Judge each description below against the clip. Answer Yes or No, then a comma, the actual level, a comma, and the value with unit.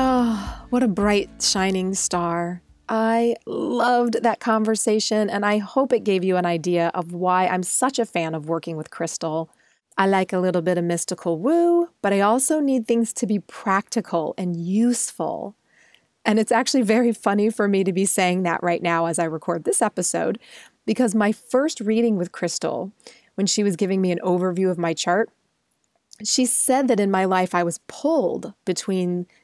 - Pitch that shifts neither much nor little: Yes, average, 4.5 semitones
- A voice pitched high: Yes, high, 200 Hz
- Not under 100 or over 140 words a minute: No, average, 185 wpm